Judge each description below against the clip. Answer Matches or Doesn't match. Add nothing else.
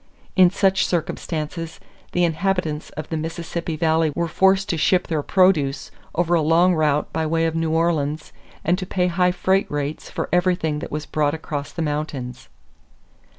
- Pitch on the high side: Doesn't match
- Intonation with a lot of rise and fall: Doesn't match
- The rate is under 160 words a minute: Doesn't match